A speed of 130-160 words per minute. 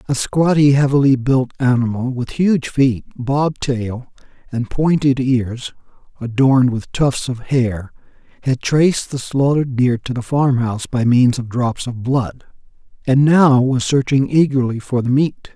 Yes: average, 155 wpm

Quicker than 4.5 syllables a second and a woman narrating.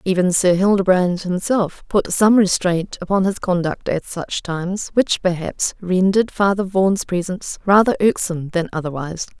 Yes: 5.0 syllables/s; female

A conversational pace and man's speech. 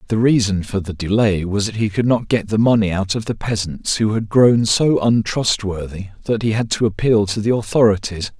No: fast, 215 wpm; male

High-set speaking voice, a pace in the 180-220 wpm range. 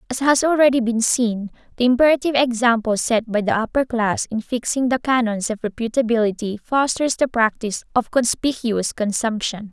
No: high, 235 Hz; average, 155 wpm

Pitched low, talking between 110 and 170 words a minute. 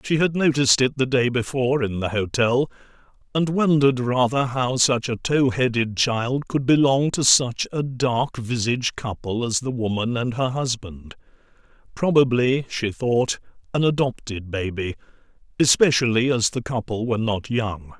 Yes: low, 125 Hz; average, 150 wpm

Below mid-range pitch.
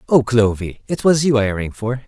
Yes: low, 120 Hz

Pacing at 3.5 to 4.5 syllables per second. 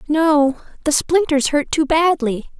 Yes: 3.8 syllables/s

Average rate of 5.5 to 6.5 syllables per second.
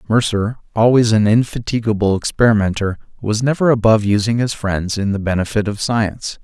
Yes: 5.8 syllables/s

